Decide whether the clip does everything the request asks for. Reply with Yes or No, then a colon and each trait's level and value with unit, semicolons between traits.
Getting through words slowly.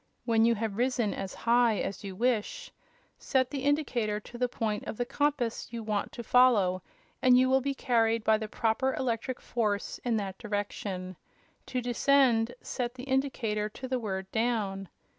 No: average, 175 wpm